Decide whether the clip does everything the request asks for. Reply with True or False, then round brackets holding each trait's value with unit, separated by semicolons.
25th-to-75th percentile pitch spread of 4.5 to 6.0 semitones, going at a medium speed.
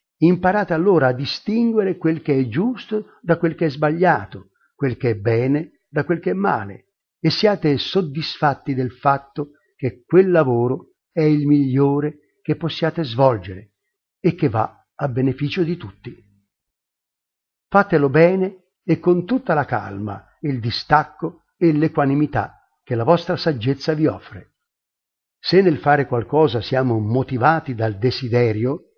True (4.9 semitones; 140 wpm)